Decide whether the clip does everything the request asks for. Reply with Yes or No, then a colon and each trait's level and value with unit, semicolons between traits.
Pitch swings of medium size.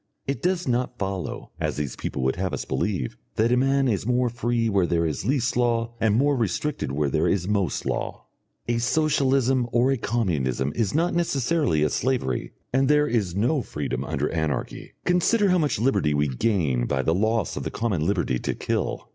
No: wide, 8.1 semitones